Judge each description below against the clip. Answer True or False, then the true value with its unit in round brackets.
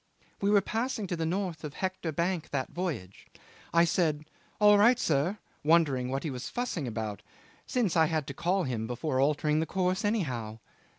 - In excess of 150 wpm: True (185 wpm)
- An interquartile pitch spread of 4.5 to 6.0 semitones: True (5.6 semitones)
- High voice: False (160 Hz)